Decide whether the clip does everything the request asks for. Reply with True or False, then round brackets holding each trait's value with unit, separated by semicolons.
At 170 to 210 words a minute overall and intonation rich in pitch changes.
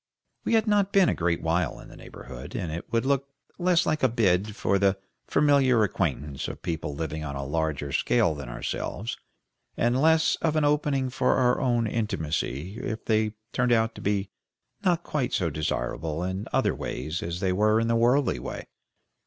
True (185 wpm; 8.1 semitones)